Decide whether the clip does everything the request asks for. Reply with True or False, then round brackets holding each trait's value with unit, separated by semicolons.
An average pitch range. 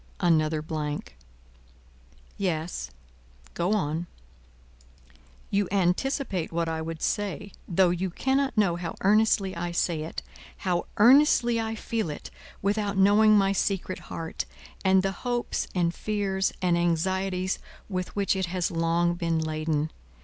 True (3.4 semitones)